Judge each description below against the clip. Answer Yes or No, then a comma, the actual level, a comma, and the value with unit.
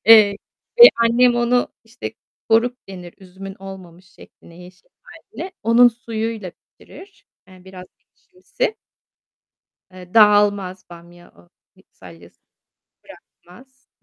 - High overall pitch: Yes, high, 200 Hz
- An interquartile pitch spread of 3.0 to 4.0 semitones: No, average, 4.7 semitones